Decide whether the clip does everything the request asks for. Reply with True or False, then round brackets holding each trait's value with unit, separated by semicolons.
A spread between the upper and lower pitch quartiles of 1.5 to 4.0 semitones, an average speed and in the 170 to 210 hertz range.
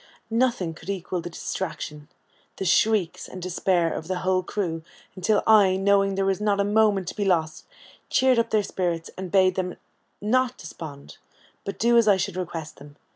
True (3.1 semitones; 180 wpm; 190 Hz)